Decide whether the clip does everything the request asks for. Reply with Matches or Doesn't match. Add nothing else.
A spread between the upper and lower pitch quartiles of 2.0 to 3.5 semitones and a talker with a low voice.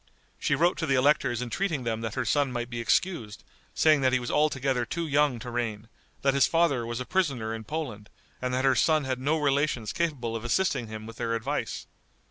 Doesn't match